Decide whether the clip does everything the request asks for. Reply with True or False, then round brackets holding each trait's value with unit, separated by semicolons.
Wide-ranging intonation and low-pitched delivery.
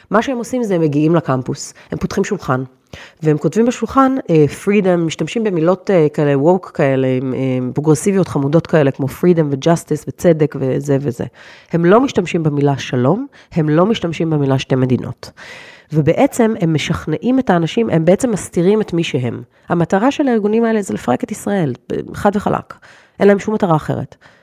False (6.3 semitones; 170 Hz)